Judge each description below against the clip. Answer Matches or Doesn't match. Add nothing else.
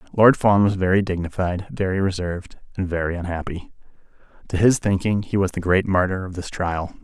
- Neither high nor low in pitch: Doesn't match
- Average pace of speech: Matches